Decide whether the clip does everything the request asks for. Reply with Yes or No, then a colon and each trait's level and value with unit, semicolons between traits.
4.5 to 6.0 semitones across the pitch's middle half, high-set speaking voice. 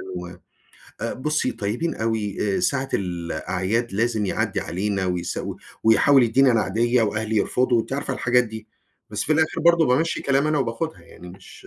No: average, 4.9 semitones; low, 115 Hz